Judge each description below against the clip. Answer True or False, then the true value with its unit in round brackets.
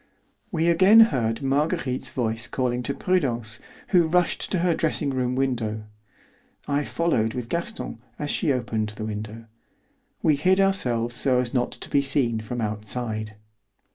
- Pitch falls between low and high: False (125 Hz)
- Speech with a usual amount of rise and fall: False (5.9 semitones)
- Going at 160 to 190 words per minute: False (150 wpm)